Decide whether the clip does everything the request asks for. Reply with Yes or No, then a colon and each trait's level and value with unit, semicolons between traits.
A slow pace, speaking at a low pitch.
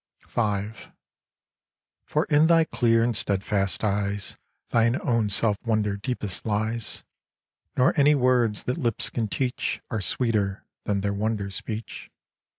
Yes: slow, 130 wpm; low, 110 Hz